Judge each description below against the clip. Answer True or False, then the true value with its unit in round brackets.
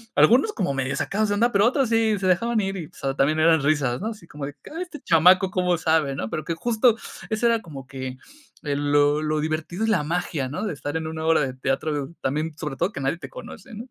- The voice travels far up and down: True (6.4 semitones)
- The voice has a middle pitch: True (160 Hz)